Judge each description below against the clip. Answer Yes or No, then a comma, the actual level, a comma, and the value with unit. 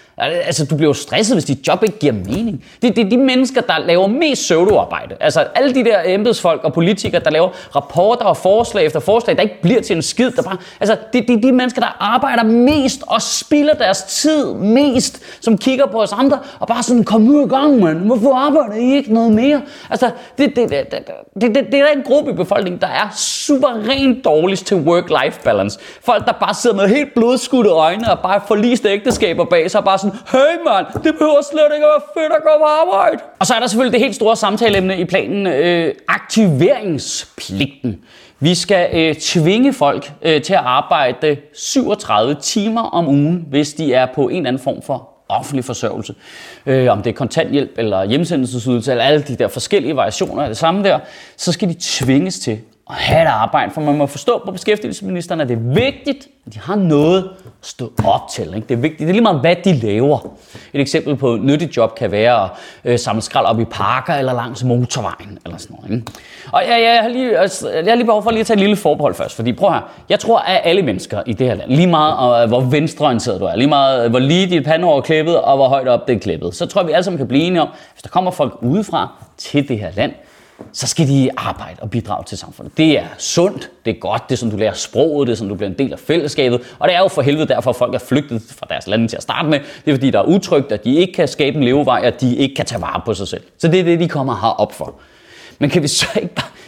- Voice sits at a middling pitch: Yes, medium, 175 Hz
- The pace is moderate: No, fast, 240 wpm